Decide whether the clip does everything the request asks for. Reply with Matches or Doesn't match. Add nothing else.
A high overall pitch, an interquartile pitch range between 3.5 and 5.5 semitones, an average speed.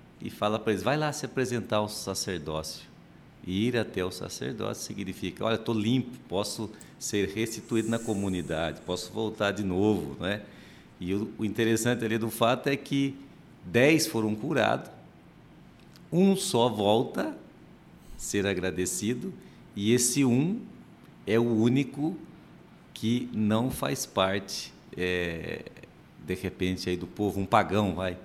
Doesn't match